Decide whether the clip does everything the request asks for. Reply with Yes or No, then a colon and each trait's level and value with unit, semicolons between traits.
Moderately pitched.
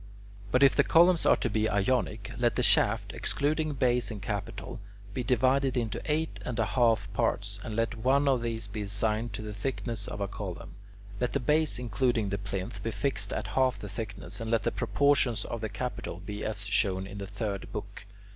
No: low, 115 Hz